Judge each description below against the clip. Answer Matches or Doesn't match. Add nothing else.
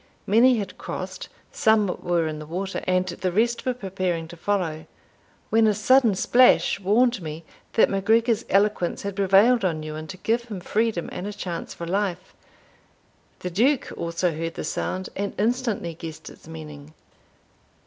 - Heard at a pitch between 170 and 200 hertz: Matches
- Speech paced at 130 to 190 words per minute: Matches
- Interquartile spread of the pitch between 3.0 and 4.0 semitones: Doesn't match